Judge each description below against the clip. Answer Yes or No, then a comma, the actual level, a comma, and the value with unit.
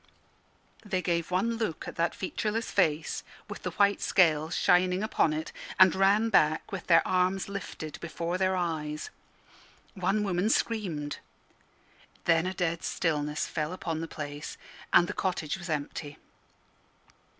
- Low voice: No, medium, 175 Hz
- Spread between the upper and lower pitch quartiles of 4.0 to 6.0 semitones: No, average, 3.4 semitones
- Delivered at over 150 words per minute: No, average, 140 wpm